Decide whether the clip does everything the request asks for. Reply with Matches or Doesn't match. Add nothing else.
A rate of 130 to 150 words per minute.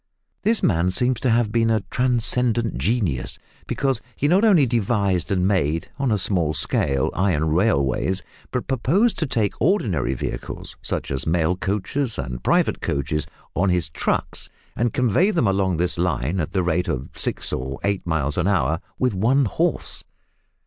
Doesn't match